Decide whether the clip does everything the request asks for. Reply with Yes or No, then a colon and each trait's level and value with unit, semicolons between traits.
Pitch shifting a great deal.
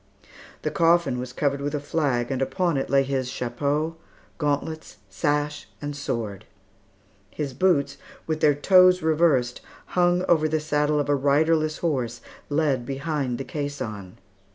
No: average, 2.8 semitones